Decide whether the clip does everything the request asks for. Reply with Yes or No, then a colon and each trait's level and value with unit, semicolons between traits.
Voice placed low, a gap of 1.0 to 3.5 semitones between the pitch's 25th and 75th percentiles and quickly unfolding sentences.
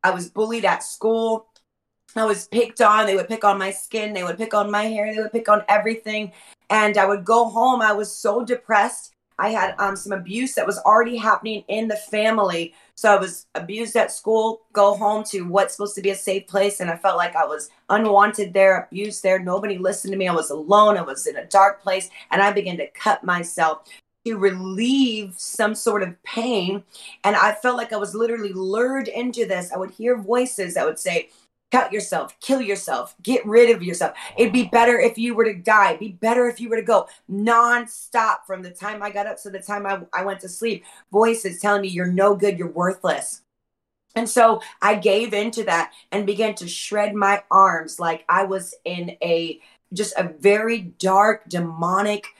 No: high, 205 Hz; average, 2.8 semitones; fast, 210 wpm